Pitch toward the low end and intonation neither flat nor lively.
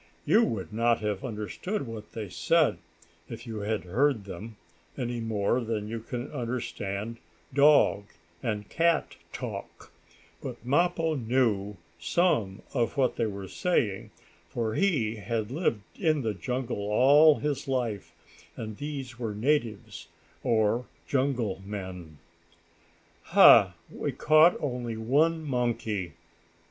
Yes: low, 115 Hz; average, 4.7 semitones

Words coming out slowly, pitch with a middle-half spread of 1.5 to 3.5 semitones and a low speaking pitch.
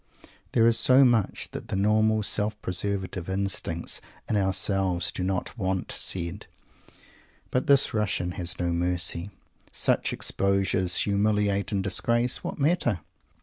Yes: slow, 130 wpm; average, 2.8 semitones; low, 100 Hz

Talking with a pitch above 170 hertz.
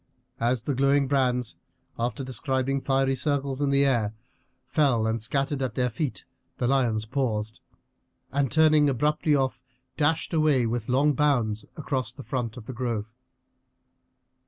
No: low, 130 Hz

